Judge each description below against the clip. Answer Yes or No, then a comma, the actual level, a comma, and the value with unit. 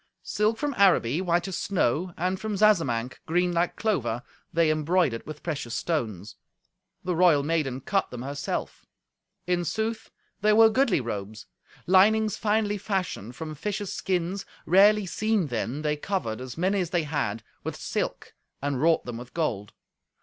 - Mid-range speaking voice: Yes, medium, 170 Hz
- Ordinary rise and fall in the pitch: No, wide, 6.6 semitones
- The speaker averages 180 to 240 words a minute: No, average, 155 wpm